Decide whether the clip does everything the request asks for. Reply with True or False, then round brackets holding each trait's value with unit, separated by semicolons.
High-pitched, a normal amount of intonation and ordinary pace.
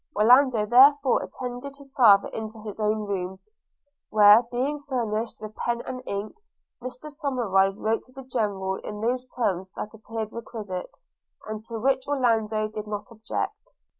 True (225 Hz; 3.2 semitones; 150 wpm)